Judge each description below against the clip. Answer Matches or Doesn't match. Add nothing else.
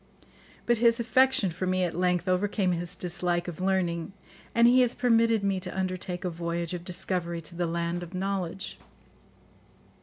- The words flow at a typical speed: Matches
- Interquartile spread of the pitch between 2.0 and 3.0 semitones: Matches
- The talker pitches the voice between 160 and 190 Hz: Matches